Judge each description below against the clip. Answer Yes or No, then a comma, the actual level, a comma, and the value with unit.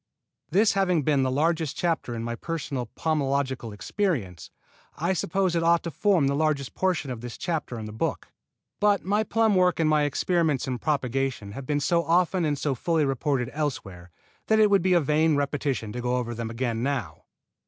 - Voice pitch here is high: No, medium, 145 Hz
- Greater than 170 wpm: Yes, average, 195 wpm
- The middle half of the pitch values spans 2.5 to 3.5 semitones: No, average, 5.3 semitones